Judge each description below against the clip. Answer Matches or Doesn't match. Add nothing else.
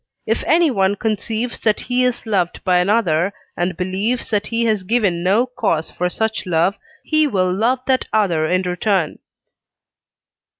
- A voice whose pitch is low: Doesn't match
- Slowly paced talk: Doesn't match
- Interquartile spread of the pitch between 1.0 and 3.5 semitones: Doesn't match